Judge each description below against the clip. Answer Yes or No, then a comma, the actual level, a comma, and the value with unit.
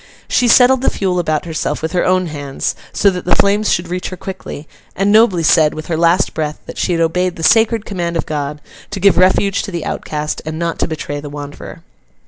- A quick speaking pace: Yes, fast, 225 wpm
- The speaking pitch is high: No, medium, 175 Hz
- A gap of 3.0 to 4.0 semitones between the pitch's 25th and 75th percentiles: Yes, average, 3.7 semitones